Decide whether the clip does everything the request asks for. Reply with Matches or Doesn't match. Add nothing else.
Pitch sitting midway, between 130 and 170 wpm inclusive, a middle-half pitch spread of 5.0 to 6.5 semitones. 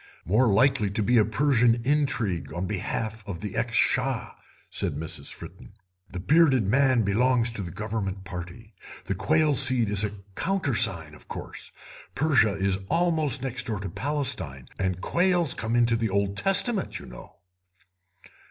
Doesn't match